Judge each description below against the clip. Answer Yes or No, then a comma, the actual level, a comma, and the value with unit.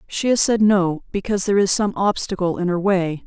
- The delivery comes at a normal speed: No, fast, 220 wpm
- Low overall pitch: No, high, 195 Hz